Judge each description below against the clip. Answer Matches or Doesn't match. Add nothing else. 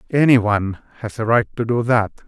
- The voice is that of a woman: Doesn't match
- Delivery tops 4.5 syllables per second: Matches